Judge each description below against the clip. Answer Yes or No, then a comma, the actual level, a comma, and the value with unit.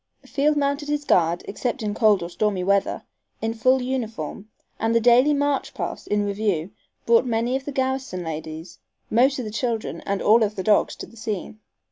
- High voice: Yes, high, 225 Hz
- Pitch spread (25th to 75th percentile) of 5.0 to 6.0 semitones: No, average, 4.6 semitones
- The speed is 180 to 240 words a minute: Yes, average, 190 wpm